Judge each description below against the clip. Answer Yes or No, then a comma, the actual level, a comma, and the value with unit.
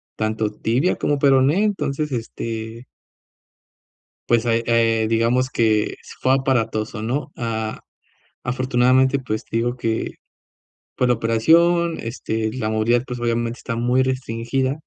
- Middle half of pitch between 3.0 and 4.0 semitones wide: No, narrow, 2.5 semitones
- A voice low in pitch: Yes, low, 120 Hz